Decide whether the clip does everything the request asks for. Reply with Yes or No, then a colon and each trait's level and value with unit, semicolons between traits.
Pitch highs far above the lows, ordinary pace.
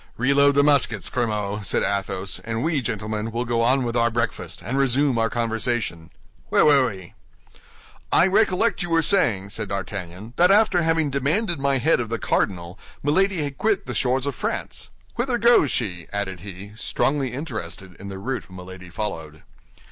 Yes: wide, 6.3 semitones; average, 170 wpm